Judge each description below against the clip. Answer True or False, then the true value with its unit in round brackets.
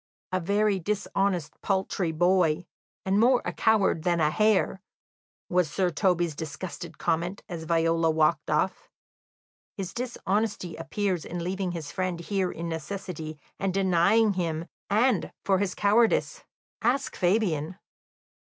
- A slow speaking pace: True (130 wpm)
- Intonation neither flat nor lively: True (3.3 semitones)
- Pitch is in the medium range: True (180 Hz)